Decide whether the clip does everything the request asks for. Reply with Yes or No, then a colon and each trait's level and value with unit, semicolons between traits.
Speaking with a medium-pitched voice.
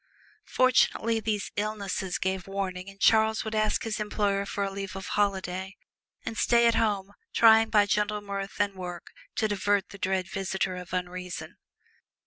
No: high, 200 Hz